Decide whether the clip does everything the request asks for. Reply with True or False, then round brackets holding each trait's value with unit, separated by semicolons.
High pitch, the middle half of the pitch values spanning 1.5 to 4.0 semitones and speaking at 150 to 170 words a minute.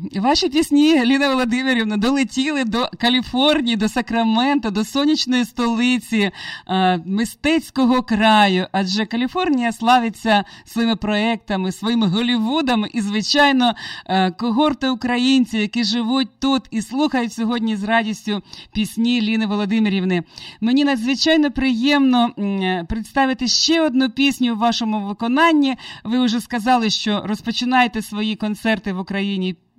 False (235 Hz; 3.5 semitones; 115 wpm)